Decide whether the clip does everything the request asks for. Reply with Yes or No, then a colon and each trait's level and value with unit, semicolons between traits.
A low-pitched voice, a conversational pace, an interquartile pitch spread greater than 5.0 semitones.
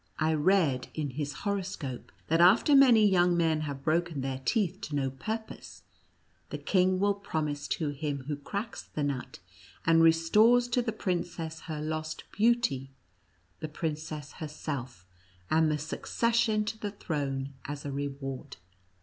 No: medium, 160 Hz; average, 150 wpm; wide, 5.5 semitones